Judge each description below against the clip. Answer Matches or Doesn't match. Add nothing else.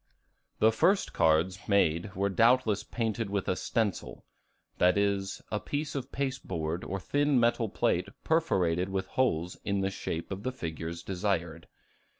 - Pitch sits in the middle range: Doesn't match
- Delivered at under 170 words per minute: Matches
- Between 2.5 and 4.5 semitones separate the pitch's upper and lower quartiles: Doesn't match